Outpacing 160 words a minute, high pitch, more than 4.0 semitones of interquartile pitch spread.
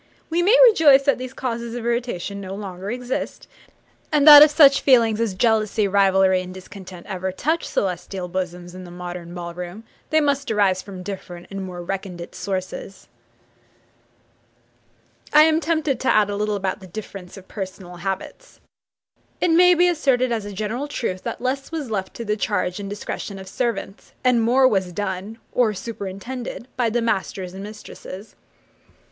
Yes: average, 170 wpm; high, 205 Hz; average, 5.2 semitones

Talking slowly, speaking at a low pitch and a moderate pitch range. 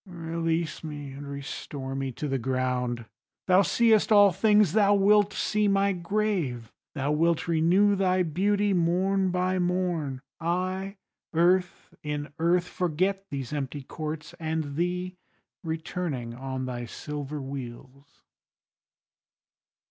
No: slow, 120 wpm; medium, 165 Hz; average, 4.9 semitones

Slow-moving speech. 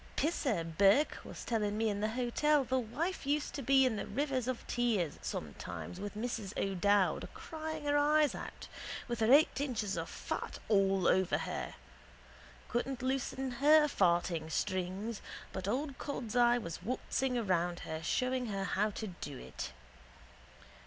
No: average, 155 wpm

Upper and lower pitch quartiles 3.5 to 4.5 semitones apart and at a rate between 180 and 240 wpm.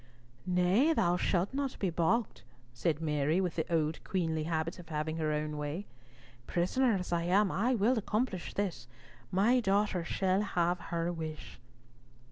No: average, 4.0 semitones; average, 155 wpm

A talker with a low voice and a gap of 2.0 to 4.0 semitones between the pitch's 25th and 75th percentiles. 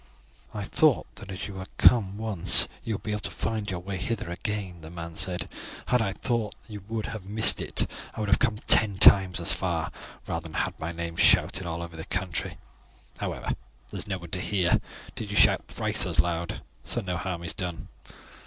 Yes: very low, 95 Hz; average, 3.5 semitones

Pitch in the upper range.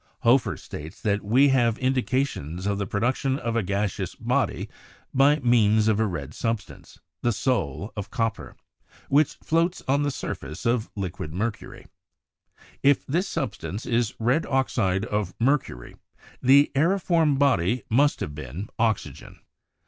No: low, 115 Hz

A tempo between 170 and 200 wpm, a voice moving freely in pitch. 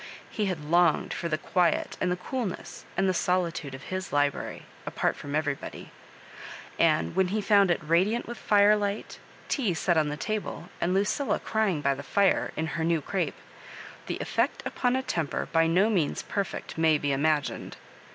No: average, 175 wpm; average, 4.5 semitones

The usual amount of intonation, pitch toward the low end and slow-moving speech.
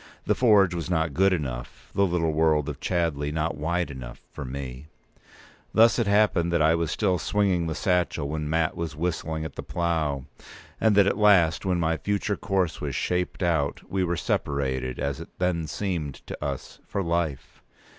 No: average, 3.5 semitones; very low, 85 Hz; average, 185 wpm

